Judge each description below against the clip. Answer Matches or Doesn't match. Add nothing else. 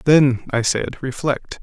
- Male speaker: Matches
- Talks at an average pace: Matches